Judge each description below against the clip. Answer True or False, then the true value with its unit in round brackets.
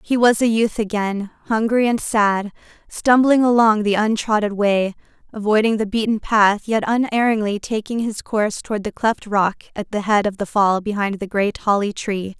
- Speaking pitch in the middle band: False (215 Hz)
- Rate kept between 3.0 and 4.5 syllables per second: False (4.9 syllables/s)